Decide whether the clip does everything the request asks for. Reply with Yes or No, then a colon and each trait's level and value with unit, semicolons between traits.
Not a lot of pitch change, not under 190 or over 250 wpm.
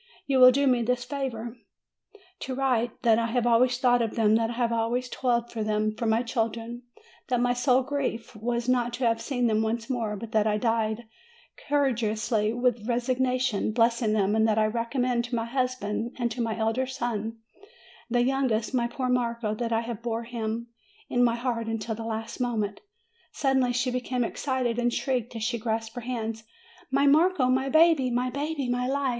Yes: narrow, 2.0 semitones; average, 195 wpm